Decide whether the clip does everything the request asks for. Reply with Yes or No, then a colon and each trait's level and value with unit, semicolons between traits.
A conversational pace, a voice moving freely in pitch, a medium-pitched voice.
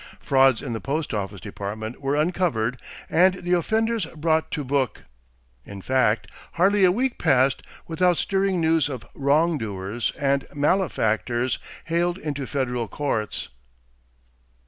No: slow, 130 wpm; wide, 6.3 semitones; medium, 145 Hz